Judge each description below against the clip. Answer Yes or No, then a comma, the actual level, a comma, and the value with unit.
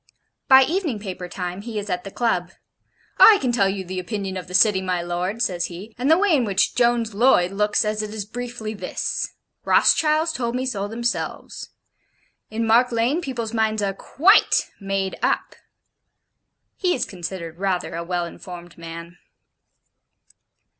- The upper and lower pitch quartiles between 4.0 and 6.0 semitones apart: Yes, average, 4.7 semitones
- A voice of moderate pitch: No, high, 210 Hz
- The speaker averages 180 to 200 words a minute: No, average, 165 wpm